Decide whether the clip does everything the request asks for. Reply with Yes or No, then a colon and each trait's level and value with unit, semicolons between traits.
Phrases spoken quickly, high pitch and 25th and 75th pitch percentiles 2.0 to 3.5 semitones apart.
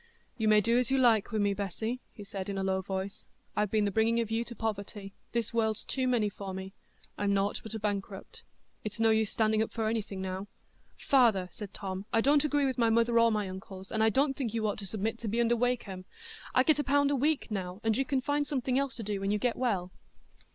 Yes: fast, 240 wpm; high, 220 Hz; average, 3.2 semitones